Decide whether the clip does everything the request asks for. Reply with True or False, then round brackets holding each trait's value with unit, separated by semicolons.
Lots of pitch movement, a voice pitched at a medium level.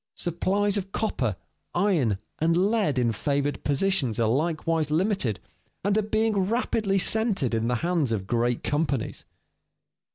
True (7.9 semitones; 165 Hz)